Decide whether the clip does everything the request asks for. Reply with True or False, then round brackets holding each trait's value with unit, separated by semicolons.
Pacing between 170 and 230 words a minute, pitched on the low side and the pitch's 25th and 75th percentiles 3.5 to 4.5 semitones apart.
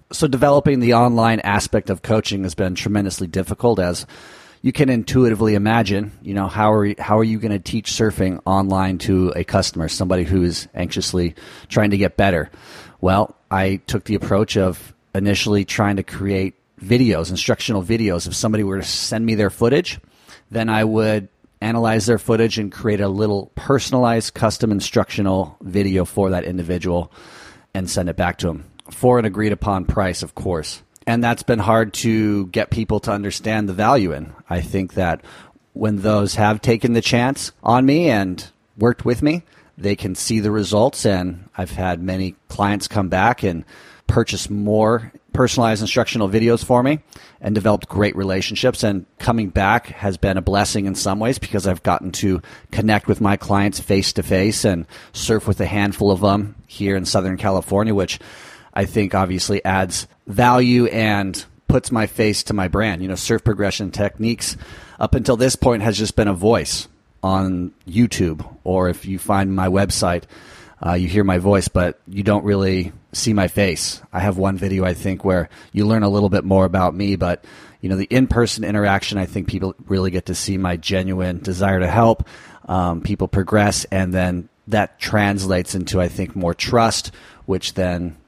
False (180 wpm; 100 Hz; 2.8 semitones)